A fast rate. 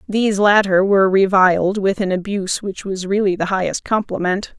No: average, 170 wpm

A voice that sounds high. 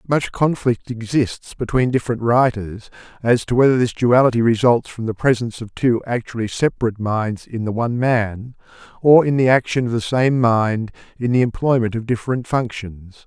No: low, 120 Hz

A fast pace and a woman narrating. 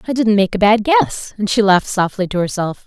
Yes: fast, 250 wpm; female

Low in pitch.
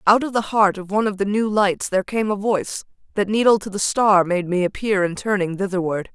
No: high, 200 Hz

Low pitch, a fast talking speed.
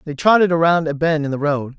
No: medium, 155 Hz; fast, 270 wpm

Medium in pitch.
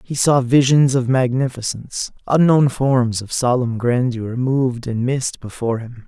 No: low, 125 Hz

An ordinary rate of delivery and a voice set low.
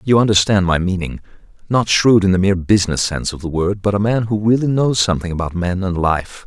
No: fast, 230 wpm; low, 100 Hz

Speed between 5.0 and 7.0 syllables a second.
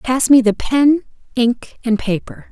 No: 3.9 syllables/s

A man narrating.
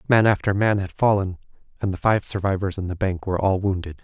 Yes: male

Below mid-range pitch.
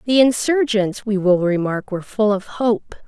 No: high, 215 Hz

